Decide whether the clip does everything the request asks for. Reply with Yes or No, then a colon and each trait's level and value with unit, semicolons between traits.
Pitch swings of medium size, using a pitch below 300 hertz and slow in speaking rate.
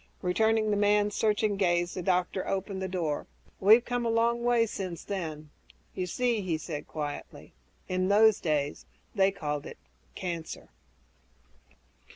No: average, 3.9 semitones; high, 190 Hz; average, 145 wpm